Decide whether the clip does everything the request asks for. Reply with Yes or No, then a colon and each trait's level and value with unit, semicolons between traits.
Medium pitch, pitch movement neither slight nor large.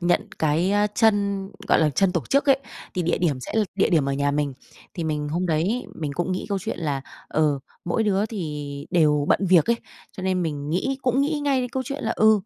No: medium, 180 Hz; wide, 5.7 semitones